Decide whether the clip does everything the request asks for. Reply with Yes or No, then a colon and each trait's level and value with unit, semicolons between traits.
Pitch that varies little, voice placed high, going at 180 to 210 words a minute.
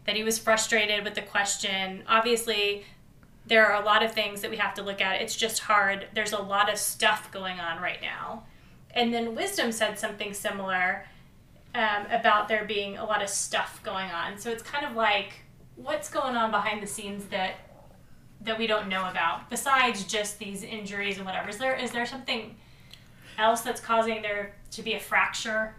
Yes: narrow, 1.8 semitones; high, 210 Hz; average, 195 wpm